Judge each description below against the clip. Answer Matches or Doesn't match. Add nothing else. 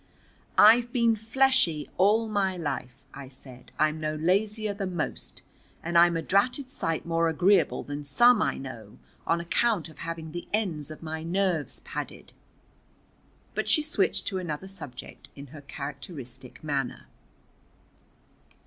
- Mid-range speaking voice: Matches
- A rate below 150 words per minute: Matches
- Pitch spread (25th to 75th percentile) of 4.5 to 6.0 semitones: Matches